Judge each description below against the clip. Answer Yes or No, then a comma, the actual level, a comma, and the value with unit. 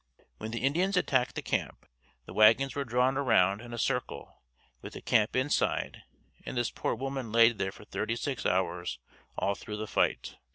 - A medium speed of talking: Yes, average, 180 wpm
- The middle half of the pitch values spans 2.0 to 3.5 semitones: No, average, 3.9 semitones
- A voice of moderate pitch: No, low, 120 Hz